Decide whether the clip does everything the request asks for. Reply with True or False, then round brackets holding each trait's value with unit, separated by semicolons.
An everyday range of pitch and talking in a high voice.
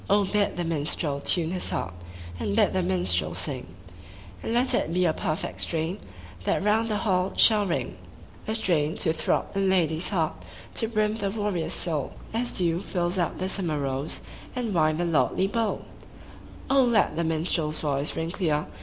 False (4.3 semitones; 175 Hz)